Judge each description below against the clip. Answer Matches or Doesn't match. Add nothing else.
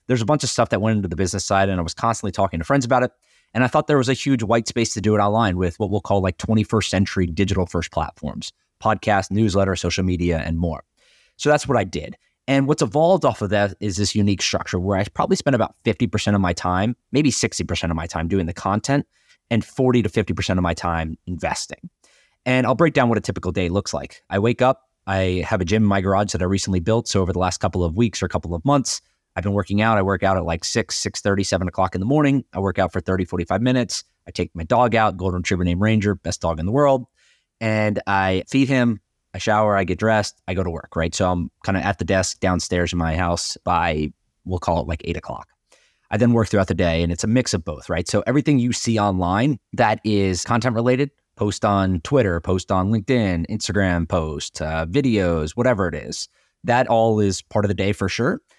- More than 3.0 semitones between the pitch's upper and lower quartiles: Matches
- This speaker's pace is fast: Matches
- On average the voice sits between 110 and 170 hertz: Doesn't match